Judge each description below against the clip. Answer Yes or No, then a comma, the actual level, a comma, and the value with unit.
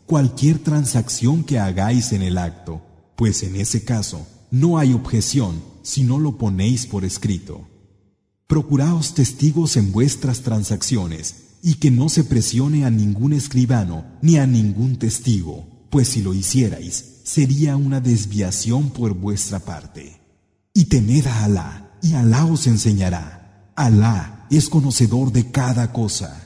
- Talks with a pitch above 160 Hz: No, low, 115 Hz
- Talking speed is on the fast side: Yes, fast, 140 wpm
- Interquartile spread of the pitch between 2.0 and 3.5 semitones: No, average, 5.3 semitones